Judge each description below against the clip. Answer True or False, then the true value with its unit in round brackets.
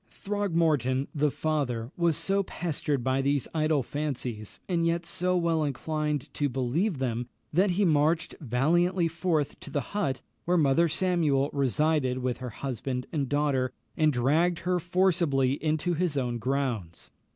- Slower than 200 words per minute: True (150 wpm)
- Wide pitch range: False (4.3 semitones)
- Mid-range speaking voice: True (150 Hz)